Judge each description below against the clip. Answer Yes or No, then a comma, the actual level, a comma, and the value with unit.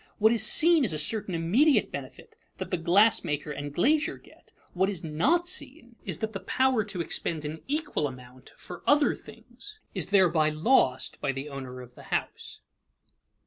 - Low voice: No, medium, 185 Hz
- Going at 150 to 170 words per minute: No, average, 180 wpm